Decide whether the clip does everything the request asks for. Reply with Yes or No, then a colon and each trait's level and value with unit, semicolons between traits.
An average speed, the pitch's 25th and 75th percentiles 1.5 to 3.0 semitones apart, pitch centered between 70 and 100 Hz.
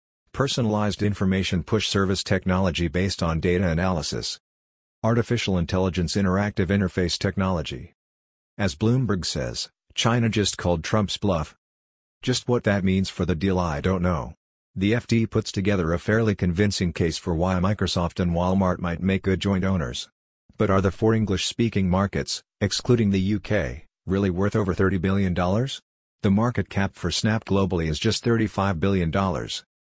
Yes: average, 150 wpm; average, 2.7 semitones; very low, 95 Hz